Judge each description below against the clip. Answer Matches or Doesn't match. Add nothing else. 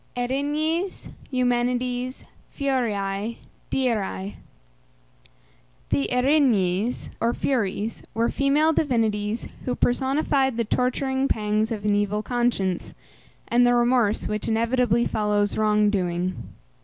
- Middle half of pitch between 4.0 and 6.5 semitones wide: Doesn't match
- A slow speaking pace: Matches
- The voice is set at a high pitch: Matches